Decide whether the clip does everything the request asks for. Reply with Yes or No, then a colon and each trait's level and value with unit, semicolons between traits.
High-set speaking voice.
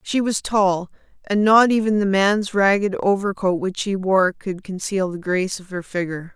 Yes: high, 195 Hz